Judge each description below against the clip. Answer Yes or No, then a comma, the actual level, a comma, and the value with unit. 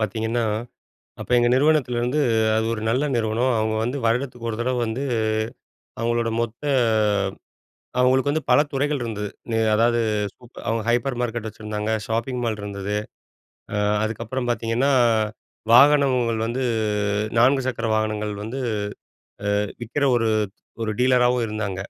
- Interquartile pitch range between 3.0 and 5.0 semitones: No, narrow, 2.5 semitones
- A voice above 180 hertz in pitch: No, low, 120 Hz